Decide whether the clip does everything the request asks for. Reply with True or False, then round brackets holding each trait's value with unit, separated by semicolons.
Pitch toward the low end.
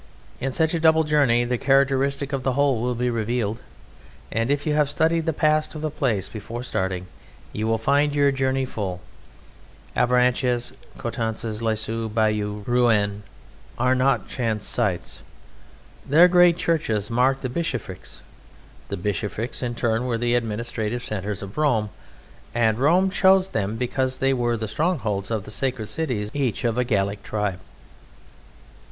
True (120 Hz)